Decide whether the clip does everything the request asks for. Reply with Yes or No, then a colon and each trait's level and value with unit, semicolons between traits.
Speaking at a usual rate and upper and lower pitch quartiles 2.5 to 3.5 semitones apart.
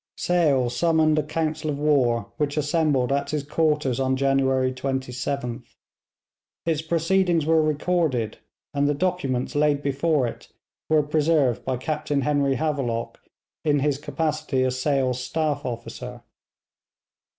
No: slow, 130 wpm; average, 3.0 semitones